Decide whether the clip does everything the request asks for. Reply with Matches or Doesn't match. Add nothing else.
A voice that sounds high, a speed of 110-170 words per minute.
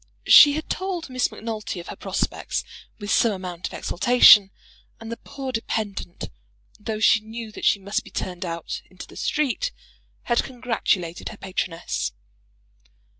Matches